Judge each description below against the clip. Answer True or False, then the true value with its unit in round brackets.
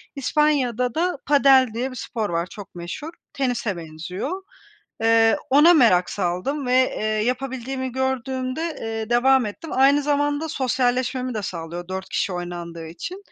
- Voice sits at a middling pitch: False (250 Hz)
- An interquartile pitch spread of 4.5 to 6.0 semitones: True (5.3 semitones)